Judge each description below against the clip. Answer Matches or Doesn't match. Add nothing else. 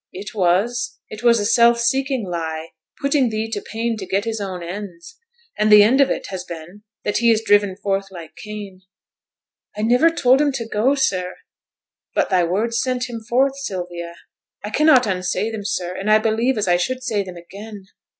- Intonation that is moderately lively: Matches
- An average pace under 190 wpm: Doesn't match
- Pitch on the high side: Matches